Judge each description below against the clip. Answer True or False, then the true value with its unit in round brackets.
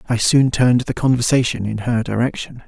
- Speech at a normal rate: True (180 wpm)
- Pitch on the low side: True (120 Hz)